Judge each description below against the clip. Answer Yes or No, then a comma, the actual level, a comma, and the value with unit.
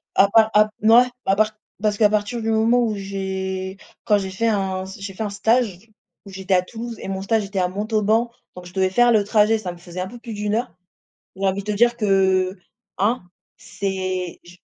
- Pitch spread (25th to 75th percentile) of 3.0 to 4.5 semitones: No, narrow, 2.6 semitones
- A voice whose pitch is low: No, high, 200 Hz